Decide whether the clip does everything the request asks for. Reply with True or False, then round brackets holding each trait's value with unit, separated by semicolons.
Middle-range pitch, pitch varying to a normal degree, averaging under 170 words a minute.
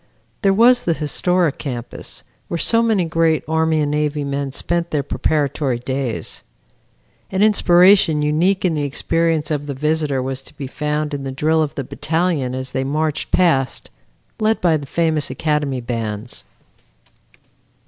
True (150 Hz; 3.4 semitones; 155 wpm)